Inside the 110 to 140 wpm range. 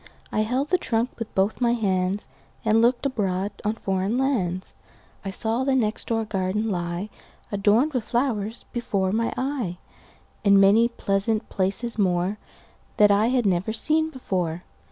Yes: slow, 135 wpm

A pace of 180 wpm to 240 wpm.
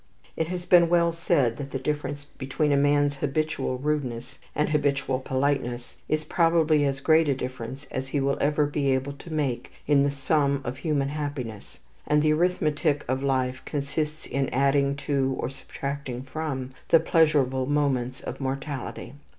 No: average, 165 wpm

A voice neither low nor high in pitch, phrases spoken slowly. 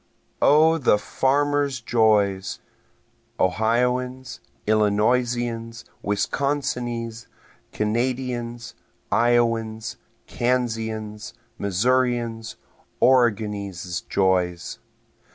No: low, 115 Hz; slow, 50 wpm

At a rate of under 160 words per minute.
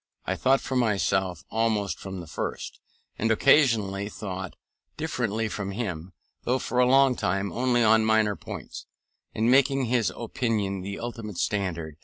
Yes: average, 150 wpm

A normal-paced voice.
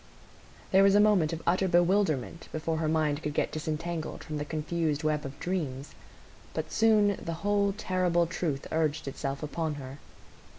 Yes: average, 165 wpm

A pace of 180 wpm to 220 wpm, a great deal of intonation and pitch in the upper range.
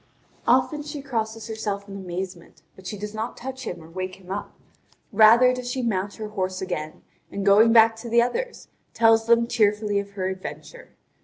No: average, 185 wpm; average, 3.5 semitones; high, 215 Hz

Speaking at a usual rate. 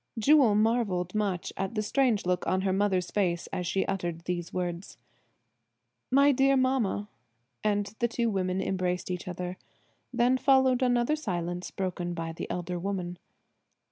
Yes: average, 150 wpm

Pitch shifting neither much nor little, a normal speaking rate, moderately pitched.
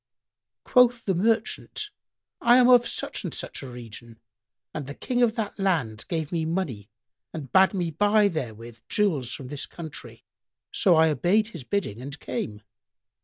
No: wide, 8.4 semitones; average, 165 wpm; medium, 165 Hz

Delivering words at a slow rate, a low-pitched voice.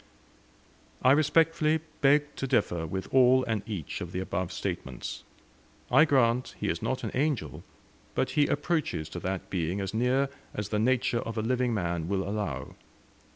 No: average, 165 wpm; low, 115 Hz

